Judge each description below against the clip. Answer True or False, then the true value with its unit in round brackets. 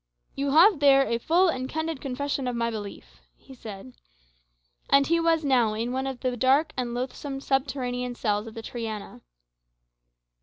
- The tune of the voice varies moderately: True (3.2 semitones)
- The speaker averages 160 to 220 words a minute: True (165 wpm)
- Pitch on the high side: True (260 Hz)